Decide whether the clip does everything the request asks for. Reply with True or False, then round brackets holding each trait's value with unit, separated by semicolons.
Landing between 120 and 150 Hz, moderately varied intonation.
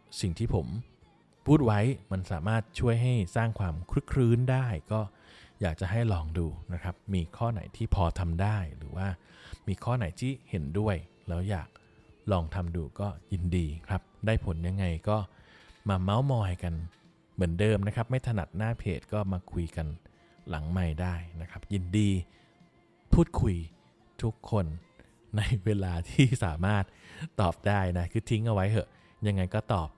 False (100 Hz; 4.0 semitones)